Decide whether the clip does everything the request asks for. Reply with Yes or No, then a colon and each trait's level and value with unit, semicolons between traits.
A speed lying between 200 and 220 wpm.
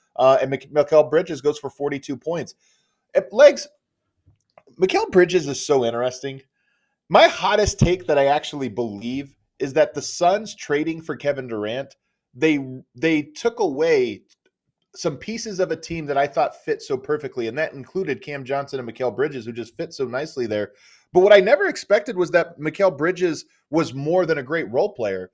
No: average, 180 wpm